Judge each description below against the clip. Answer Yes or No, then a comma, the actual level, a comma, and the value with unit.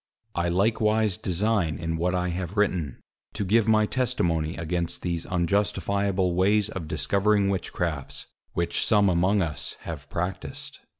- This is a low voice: Yes, very low, 90 Hz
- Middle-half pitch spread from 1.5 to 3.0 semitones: No, average, 3.4 semitones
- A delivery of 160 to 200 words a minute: No, slow, 135 wpm